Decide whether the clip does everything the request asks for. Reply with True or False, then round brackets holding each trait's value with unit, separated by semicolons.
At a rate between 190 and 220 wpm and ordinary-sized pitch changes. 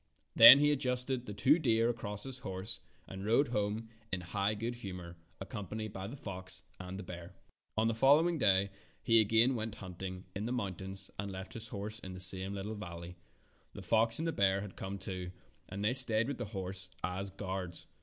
True (200 wpm; 3.4 semitones)